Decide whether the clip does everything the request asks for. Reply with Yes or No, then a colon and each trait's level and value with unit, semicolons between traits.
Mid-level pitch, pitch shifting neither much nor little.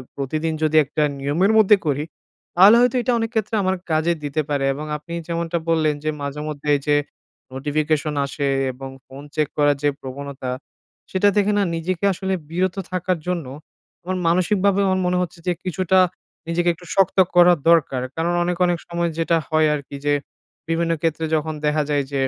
Yes: medium, 165 Hz; average, 3.5 semitones